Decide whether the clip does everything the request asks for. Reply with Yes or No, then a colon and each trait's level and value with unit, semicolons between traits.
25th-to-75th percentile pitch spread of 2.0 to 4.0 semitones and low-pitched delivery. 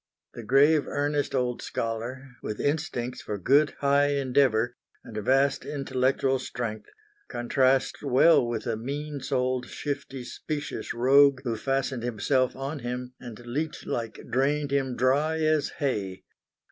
Yes: average, 2.7 semitones; low, 130 Hz